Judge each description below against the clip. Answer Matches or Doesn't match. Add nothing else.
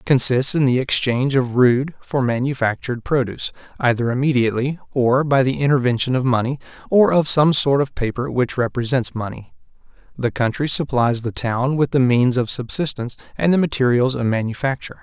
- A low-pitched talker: Matches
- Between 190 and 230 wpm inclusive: Doesn't match